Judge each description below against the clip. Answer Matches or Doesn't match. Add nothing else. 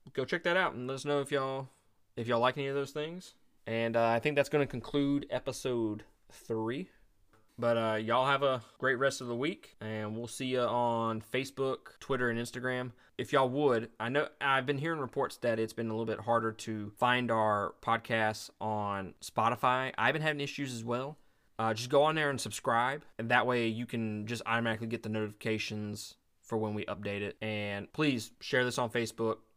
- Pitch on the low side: Matches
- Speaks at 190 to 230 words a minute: Matches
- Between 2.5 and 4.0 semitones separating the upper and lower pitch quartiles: Matches